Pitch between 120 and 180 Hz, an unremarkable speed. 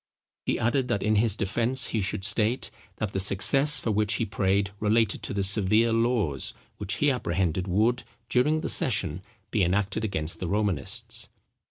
No: low, 105 Hz; average, 170 wpm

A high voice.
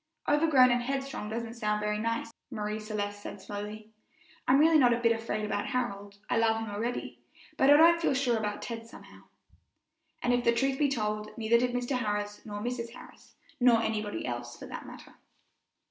Yes: high, 230 Hz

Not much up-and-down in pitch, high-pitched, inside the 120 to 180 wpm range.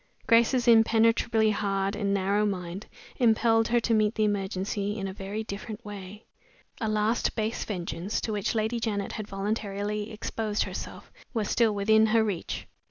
Yes: narrow, 1.9 semitones; high, 210 Hz; average, 160 wpm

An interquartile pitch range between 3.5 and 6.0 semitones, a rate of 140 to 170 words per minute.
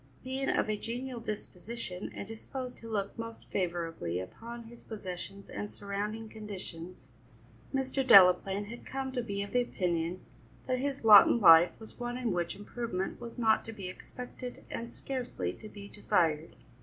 Yes: average, 4.6 semitones; average, 165 wpm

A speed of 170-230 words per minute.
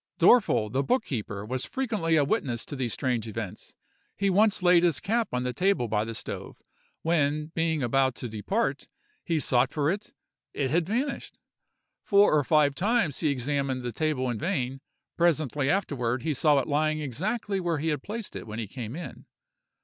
Yes: average, 185 wpm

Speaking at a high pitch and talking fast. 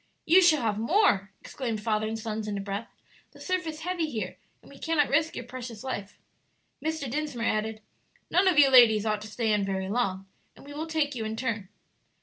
Yes: high, 235 Hz; fast, 210 wpm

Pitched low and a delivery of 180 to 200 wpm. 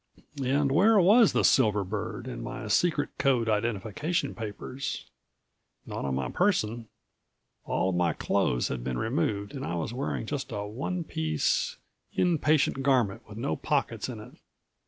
No: low, 120 Hz; average, 155 wpm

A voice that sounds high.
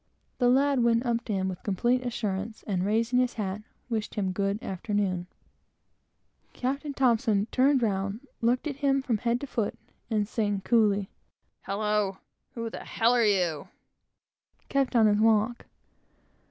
Yes: high, 220 Hz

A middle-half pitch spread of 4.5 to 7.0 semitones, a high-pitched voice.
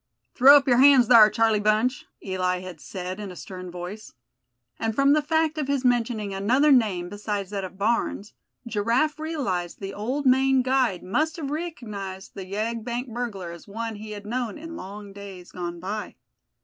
Yes: average, 5.0 semitones; high, 215 Hz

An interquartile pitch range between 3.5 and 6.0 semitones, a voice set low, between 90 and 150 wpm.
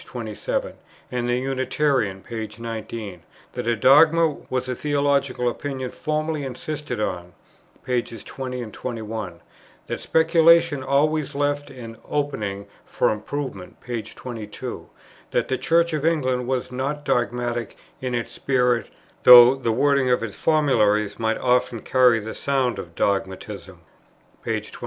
Yes: average, 4.1 semitones; low, 125 Hz; slow, 135 wpm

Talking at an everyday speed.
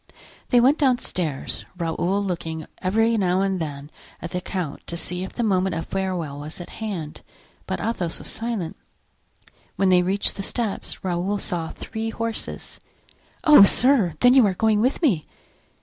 Yes: average, 165 wpm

